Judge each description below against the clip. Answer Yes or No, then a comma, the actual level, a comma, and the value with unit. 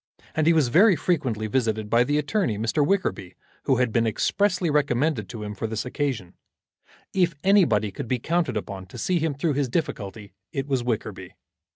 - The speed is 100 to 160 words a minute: No, average, 185 wpm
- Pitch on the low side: Yes, low, 130 Hz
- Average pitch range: No, wide, 6.6 semitones